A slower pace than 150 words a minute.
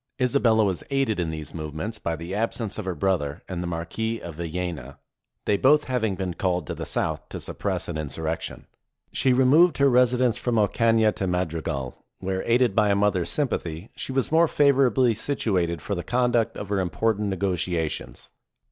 No: average, 180 wpm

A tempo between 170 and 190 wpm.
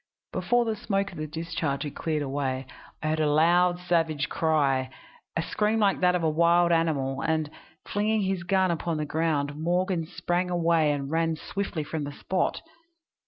Yes: average, 175 wpm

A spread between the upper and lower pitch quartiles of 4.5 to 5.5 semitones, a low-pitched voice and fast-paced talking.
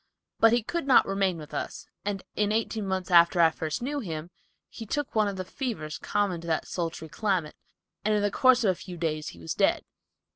No: average, 4.8 semitones; high, 190 Hz; fast, 220 wpm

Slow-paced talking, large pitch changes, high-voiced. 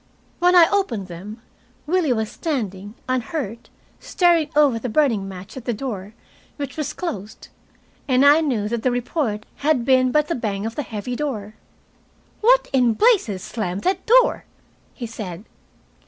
No: average, 155 wpm; wide, 6.2 semitones; very high, 250 Hz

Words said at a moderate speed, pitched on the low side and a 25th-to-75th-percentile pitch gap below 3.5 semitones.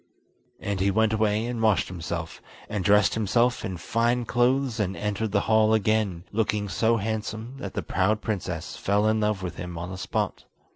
Yes: average, 185 wpm; low, 105 Hz; average, 2.7 semitones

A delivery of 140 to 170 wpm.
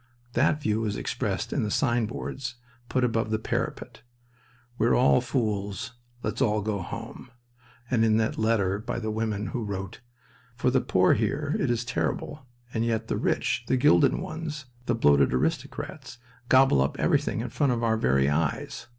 Yes: average, 165 wpm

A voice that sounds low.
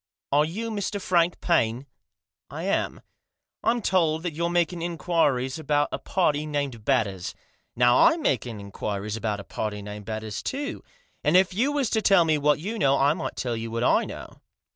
No: medium, 150 Hz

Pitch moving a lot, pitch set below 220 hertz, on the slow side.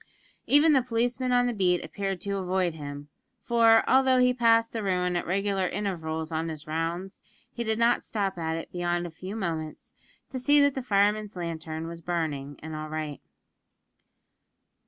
No: wide, 5.8 semitones; high, 190 Hz; average, 175 wpm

